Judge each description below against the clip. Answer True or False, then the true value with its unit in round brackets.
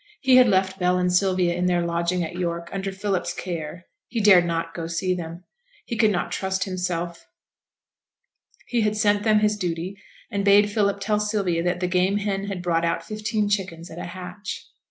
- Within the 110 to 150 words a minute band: False (195 wpm)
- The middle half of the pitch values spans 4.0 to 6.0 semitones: False (3.0 semitones)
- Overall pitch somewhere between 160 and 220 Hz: True (185 Hz)